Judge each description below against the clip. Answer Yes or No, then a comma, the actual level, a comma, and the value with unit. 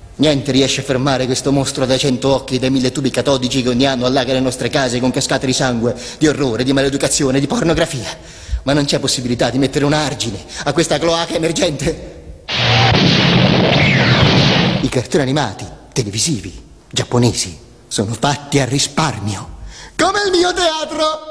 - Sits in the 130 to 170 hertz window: Yes, low, 135 Hz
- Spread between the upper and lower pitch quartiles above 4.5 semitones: No, average, 2.8 semitones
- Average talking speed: Yes, average, 160 wpm